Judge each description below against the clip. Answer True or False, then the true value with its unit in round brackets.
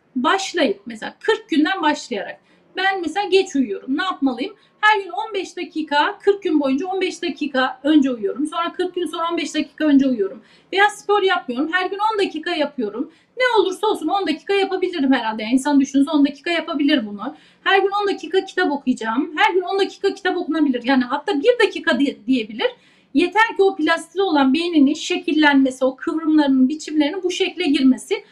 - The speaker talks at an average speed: False (170 wpm)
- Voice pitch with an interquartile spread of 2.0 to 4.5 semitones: False (5.2 semitones)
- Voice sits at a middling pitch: False (325 Hz)